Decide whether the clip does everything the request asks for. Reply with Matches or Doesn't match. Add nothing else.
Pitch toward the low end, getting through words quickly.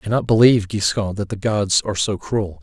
Matches